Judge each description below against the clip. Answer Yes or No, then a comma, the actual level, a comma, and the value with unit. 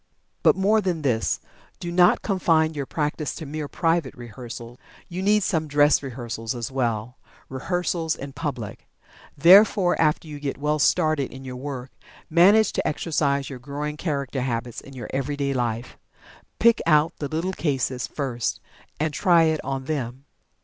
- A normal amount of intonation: Yes, average, 3.9 semitones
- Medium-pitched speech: Yes, medium, 145 Hz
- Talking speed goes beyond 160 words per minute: No, average, 155 wpm